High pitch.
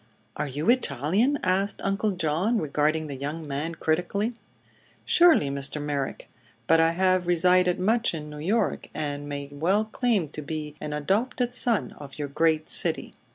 No: medium, 165 Hz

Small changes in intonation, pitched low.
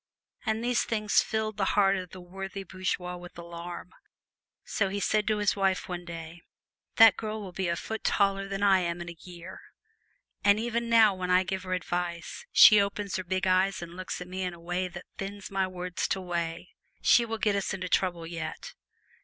No: narrow, 2.3 semitones; medium, 185 Hz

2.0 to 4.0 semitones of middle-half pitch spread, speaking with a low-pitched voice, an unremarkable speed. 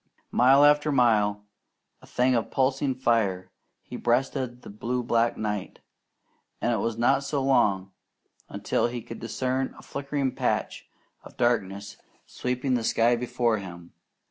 Yes: average, 3.2 semitones; low, 120 Hz; average, 145 wpm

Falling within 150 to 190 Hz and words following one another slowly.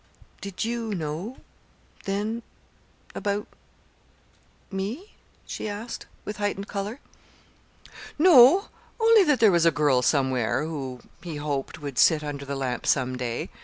Yes: medium, 185 Hz; slow, 130 wpm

